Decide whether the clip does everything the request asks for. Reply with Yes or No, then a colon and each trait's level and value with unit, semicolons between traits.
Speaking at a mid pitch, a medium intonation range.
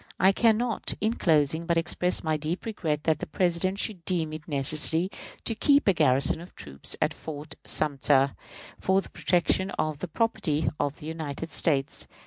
Yes: medium, 160 Hz; average, 3.8 semitones